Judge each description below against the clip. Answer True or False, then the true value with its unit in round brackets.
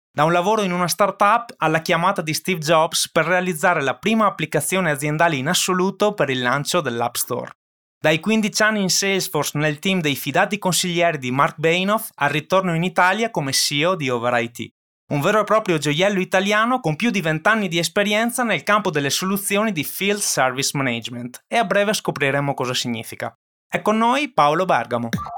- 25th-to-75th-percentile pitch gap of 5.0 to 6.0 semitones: True (5.5 semitones)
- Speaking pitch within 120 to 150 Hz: False (175 Hz)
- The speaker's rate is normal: False (180 wpm)